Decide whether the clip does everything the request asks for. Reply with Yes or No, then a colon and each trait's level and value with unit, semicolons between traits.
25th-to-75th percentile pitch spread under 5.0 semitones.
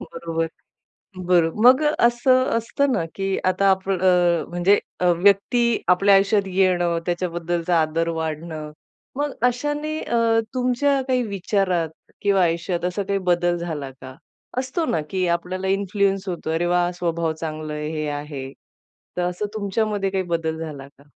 Yes: average, 3.3 semitones